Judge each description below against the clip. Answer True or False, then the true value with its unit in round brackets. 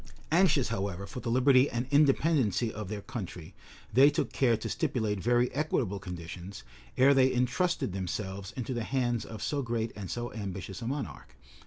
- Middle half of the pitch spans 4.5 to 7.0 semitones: True (4.9 semitones)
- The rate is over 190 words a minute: False (170 wpm)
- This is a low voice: True (120 Hz)